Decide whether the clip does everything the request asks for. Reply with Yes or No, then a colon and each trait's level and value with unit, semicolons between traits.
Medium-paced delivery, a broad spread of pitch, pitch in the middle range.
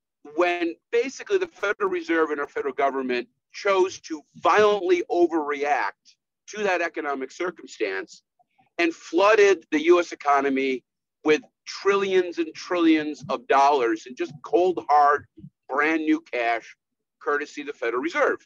No: slow, 130 wpm; wide, 5.7 semitones; medium, 165 Hz